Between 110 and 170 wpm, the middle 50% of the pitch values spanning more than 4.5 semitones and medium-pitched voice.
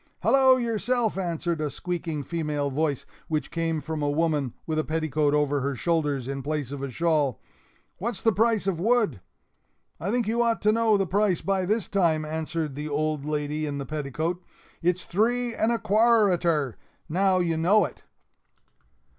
No: average, 180 wpm; average, 5.3 semitones; medium, 165 Hz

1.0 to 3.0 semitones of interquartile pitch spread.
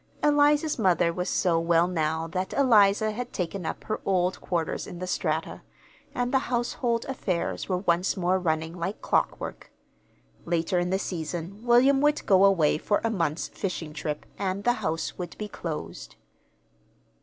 No: average, 4.5 semitones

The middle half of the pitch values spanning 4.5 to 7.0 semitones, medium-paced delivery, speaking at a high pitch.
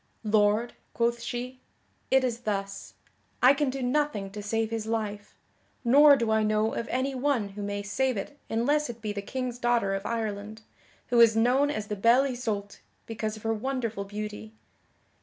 No: average, 3.3 semitones; average, 175 wpm; high, 225 Hz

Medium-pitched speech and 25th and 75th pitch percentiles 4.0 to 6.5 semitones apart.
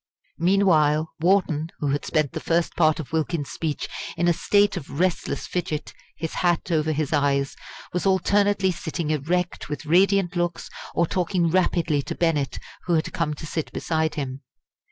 No: medium, 165 Hz; average, 2.8 semitones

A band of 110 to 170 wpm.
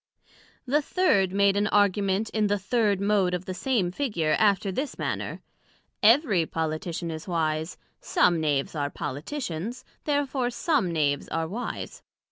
Yes: average, 140 wpm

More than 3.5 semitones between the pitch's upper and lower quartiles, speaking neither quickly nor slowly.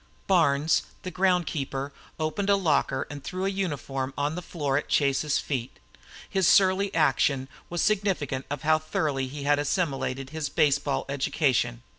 Yes: average, 4.5 semitones; average, 155 wpm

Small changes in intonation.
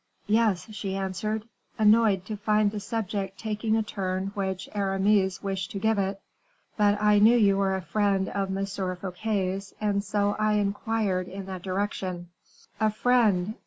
Yes: narrow, 1.8 semitones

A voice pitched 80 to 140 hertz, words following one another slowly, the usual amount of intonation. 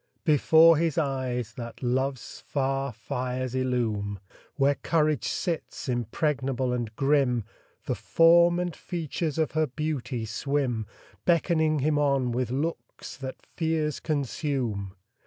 Yes: low, 135 Hz; slow, 120 wpm; average, 4.0 semitones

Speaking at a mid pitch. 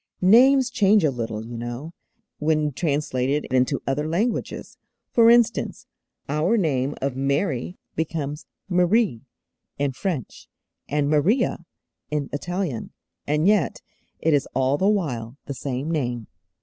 Yes: medium, 150 Hz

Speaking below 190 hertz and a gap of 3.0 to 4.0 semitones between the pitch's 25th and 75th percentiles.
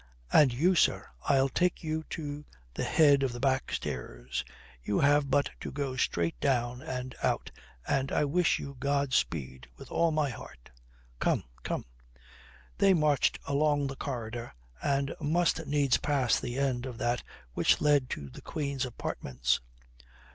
Yes: low, 135 Hz; average, 3.3 semitones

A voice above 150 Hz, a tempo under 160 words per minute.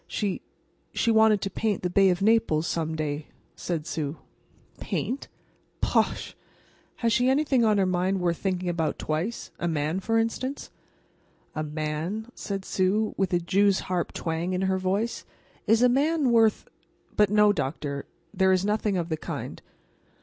Yes: high, 190 Hz; average, 150 wpm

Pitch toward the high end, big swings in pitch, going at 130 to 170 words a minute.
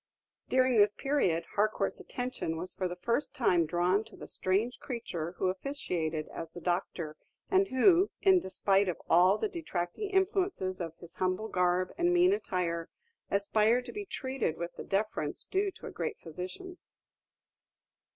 Yes: high, 200 Hz; wide, 7.9 semitones; average, 160 wpm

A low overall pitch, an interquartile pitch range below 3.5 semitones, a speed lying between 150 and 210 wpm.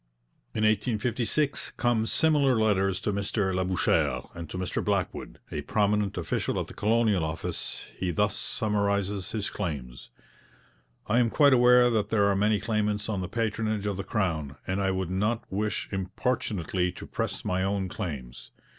Yes: low, 100 Hz; average, 3.0 semitones; average, 160 wpm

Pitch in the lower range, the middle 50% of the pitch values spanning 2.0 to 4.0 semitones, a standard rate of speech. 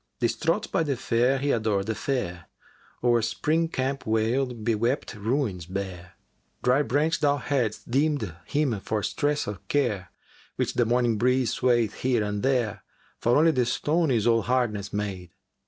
No: low, 120 Hz; average, 4.5 semitones; average, 170 wpm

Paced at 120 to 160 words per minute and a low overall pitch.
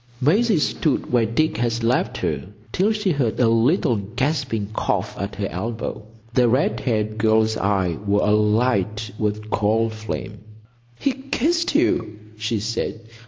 Yes: average, 145 wpm; low, 115 Hz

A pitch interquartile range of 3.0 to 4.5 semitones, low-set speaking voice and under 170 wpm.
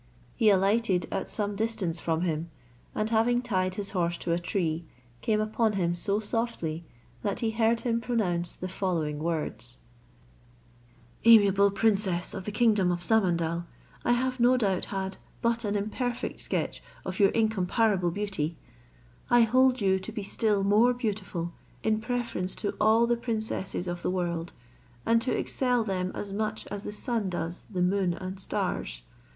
No: average, 4.1 semitones; high, 200 Hz; average, 160 wpm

